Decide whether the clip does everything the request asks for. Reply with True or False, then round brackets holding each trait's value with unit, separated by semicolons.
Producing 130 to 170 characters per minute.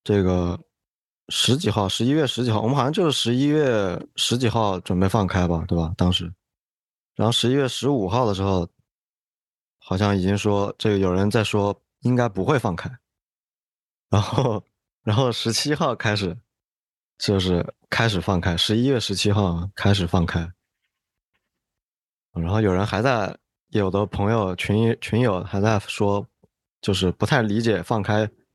False (230 characters per minute)